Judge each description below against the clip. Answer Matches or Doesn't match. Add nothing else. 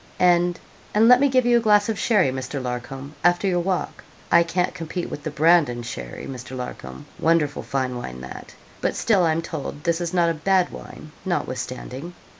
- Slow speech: Doesn't match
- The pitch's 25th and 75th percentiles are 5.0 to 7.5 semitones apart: Matches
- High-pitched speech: Doesn't match